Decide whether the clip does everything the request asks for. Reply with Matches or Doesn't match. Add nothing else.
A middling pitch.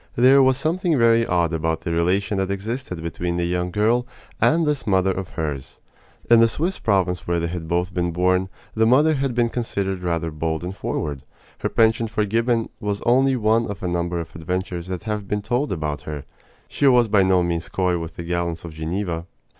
Doesn't match